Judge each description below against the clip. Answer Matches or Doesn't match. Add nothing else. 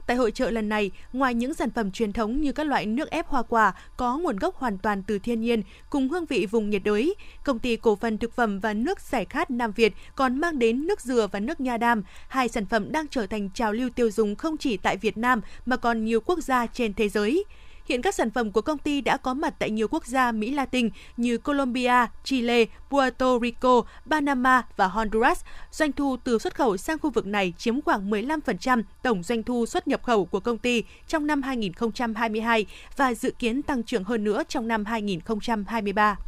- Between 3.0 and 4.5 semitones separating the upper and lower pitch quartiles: Matches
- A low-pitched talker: Doesn't match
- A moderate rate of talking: Matches